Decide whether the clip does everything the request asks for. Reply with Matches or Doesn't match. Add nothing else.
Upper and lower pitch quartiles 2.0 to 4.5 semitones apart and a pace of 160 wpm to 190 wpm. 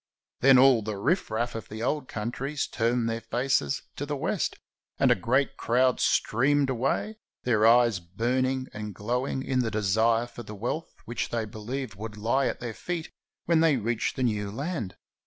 Matches